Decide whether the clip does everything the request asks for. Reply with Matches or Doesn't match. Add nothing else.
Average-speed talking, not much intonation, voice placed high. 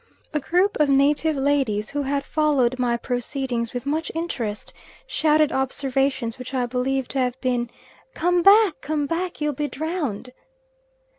Doesn't match